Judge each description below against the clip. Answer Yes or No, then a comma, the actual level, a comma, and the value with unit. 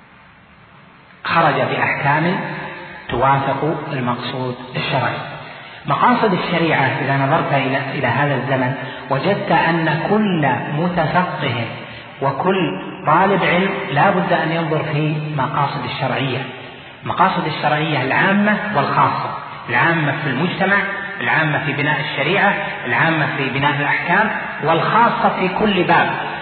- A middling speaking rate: Yes, average, 100 wpm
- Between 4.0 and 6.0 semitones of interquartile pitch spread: Yes, average, 4.7 semitones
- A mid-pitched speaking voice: Yes, medium, 155 Hz